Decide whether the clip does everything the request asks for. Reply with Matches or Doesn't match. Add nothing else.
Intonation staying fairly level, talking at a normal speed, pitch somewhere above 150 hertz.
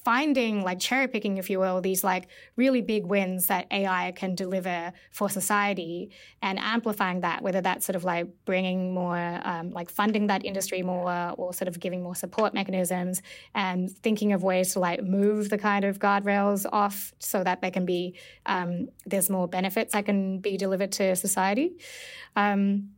Matches